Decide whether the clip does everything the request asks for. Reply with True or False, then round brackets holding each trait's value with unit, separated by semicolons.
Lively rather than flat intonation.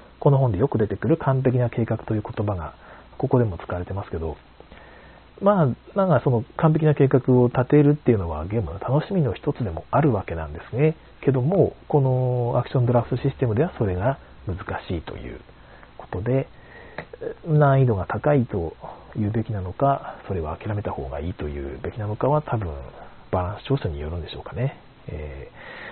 True (6.9 semitones)